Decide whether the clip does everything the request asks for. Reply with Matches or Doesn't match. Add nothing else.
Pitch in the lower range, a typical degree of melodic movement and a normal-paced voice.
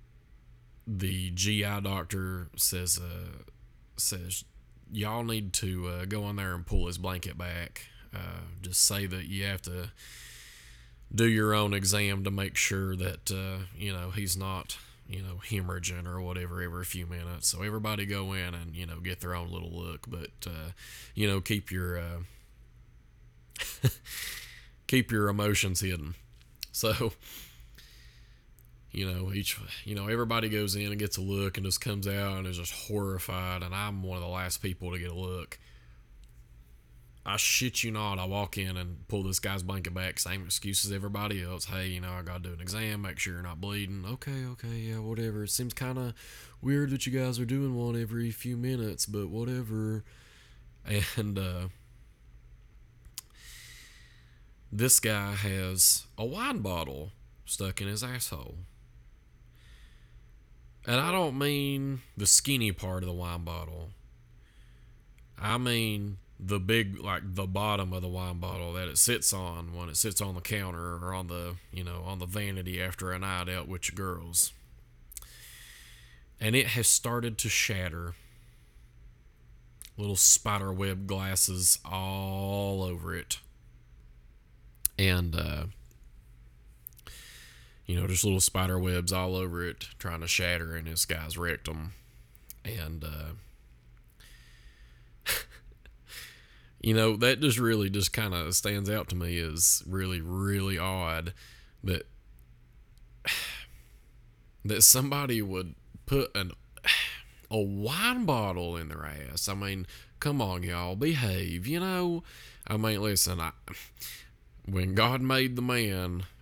Matches